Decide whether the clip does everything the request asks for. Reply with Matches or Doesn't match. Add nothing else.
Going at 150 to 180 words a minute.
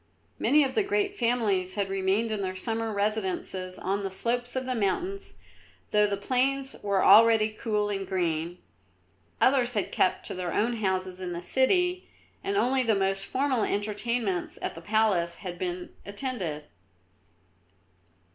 Matches